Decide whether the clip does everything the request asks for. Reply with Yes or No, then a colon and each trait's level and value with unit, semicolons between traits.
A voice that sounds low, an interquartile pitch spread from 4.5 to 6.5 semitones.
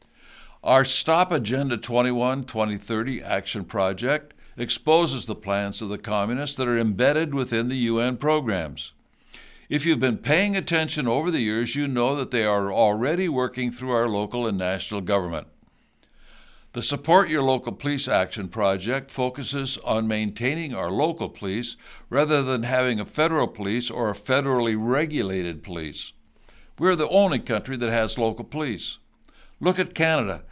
Yes: low, 125 Hz; average, 4.9 semitones